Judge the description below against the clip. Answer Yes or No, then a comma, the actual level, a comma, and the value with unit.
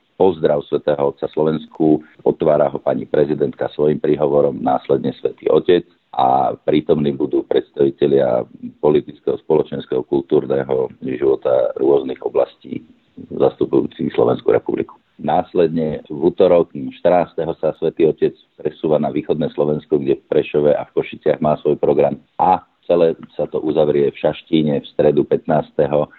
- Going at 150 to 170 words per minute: No, average, 130 wpm